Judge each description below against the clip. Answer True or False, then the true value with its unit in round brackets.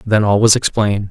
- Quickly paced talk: True (215 wpm)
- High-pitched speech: False (105 Hz)